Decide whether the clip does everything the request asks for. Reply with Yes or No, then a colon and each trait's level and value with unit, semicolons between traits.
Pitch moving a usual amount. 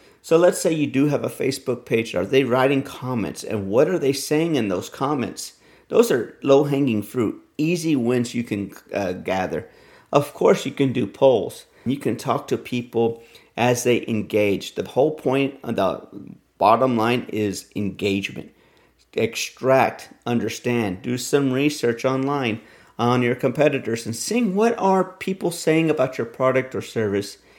Yes: average, 3.8 semitones